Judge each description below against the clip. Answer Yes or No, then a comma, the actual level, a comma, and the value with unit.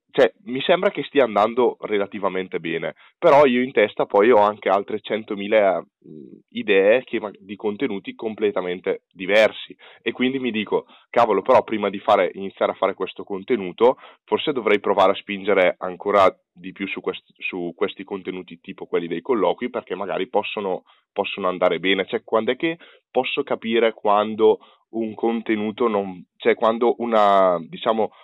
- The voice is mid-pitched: No, low, 110 Hz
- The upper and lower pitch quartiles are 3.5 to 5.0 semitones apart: Yes, average, 4.2 semitones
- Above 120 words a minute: Yes, average, 155 wpm